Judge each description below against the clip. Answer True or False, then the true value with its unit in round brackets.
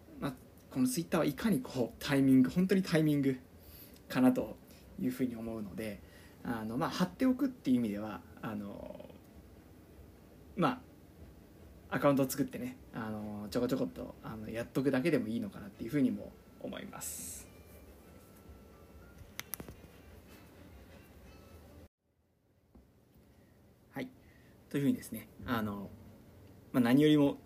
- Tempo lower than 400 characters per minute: True (270 characters per minute)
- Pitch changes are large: True (7.4 semitones)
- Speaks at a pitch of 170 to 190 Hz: False (100 Hz)